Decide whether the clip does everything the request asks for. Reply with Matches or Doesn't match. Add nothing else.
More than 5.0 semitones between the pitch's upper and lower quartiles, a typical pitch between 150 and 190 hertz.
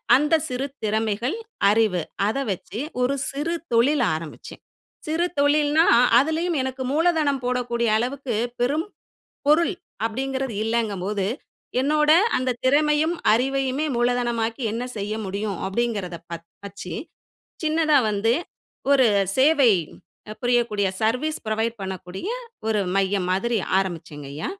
Doesn't match